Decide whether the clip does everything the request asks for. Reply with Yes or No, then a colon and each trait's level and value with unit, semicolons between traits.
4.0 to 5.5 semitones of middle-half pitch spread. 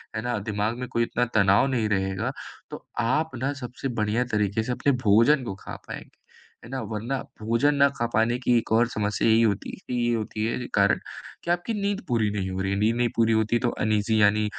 No: average, 2.7 semitones